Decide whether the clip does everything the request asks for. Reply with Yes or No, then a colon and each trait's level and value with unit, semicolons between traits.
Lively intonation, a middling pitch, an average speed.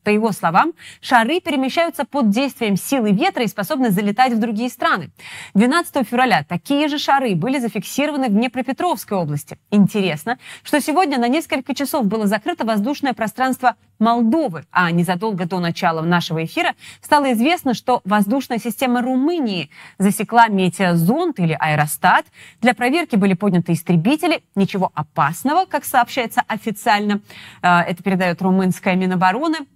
No: wide, 6.4 semitones; high, 225 Hz; average, 135 wpm